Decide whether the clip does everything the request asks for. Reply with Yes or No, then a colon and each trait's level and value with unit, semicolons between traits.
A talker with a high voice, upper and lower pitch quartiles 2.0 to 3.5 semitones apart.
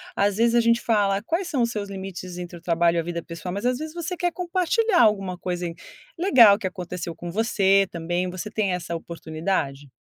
No: high, 195 Hz; average, 5.1 semitones